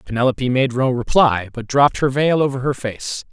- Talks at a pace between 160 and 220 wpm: Yes, average, 200 wpm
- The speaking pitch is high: No, low, 130 Hz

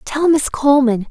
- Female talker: Yes, female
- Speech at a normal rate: Yes, average, 165 wpm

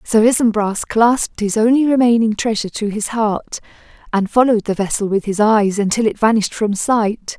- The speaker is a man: No, female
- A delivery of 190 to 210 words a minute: No, average, 180 wpm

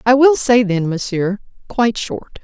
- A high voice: Yes, high, 220 Hz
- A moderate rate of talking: Yes, average, 175 wpm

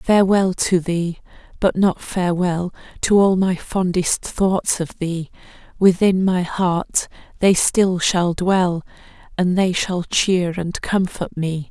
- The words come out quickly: No, average, 140 wpm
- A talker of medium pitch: Yes, medium, 180 Hz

